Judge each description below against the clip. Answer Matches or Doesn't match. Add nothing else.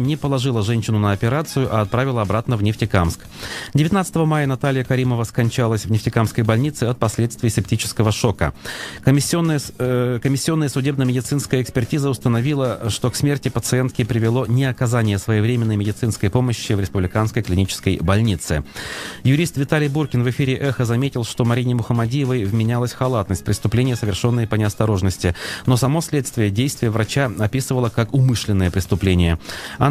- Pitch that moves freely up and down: Doesn't match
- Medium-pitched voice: Doesn't match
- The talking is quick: Doesn't match